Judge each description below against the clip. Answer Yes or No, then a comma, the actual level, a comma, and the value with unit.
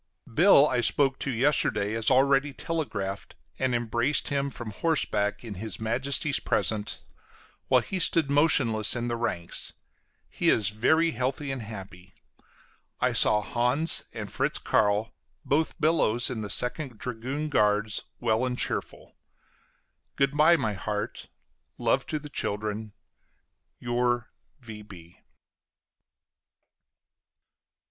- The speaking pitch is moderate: No, low, 120 Hz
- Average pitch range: Yes, average, 4.6 semitones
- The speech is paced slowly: Yes, slow, 120 wpm